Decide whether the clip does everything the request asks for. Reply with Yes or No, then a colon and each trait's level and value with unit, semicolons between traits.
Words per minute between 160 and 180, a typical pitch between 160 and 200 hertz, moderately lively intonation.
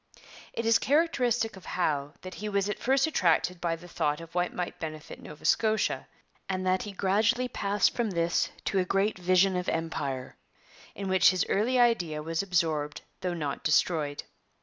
Yes: average, 175 wpm; medium, 185 Hz; average, 4.2 semitones